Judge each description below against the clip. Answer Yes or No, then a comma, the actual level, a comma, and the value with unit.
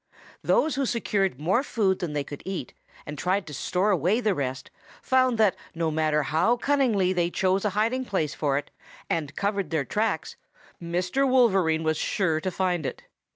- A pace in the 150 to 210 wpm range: Yes, average, 180 wpm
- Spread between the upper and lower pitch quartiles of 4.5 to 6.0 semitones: Yes, average, 5.2 semitones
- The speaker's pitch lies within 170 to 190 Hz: Yes, medium, 185 Hz